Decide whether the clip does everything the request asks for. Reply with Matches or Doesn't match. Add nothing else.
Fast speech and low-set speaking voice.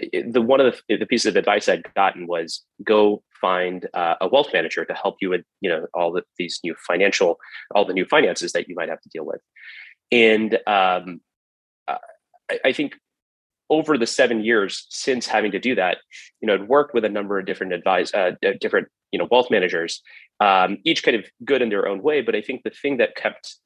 Matches